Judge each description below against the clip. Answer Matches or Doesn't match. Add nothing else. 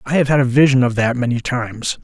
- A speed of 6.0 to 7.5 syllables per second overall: Matches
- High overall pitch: Doesn't match